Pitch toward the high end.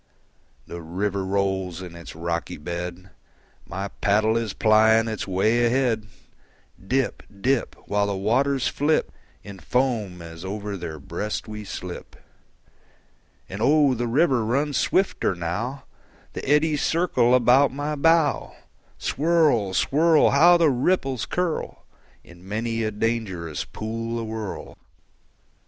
No: low, 110 Hz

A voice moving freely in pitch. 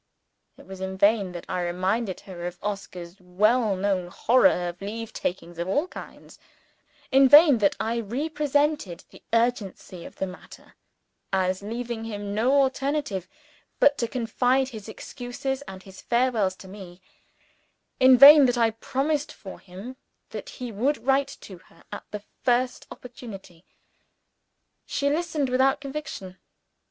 Yes: wide, 5.7 semitones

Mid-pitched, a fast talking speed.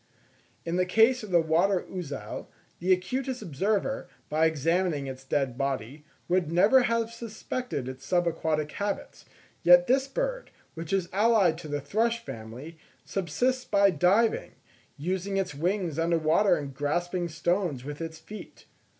No: medium, 175 Hz; average, 145 wpm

